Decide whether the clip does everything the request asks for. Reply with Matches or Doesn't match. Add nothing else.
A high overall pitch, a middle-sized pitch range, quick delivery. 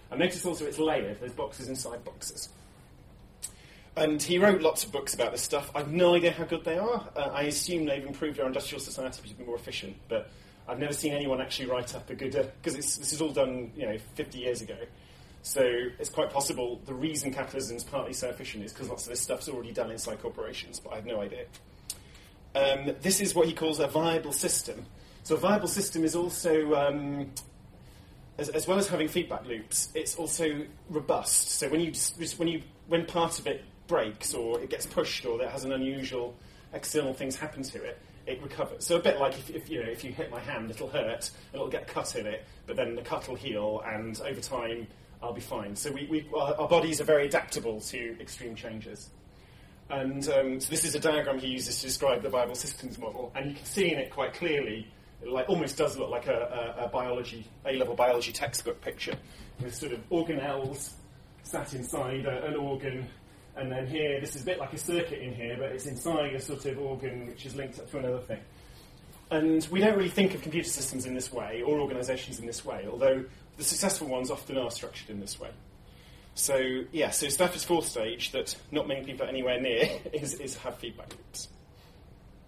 Doesn't match